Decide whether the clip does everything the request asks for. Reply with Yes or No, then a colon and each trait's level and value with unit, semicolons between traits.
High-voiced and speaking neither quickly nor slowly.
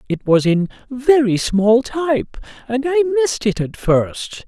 Yes: high, 245 Hz; average, 160 wpm